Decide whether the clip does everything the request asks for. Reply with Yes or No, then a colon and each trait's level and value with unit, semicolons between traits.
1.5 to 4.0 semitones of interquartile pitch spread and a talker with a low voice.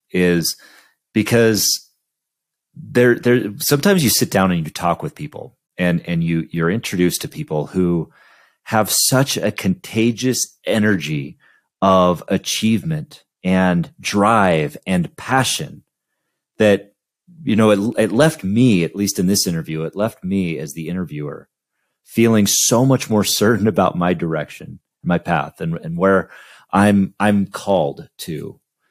No: average, 5.2 semitones; low, 100 Hz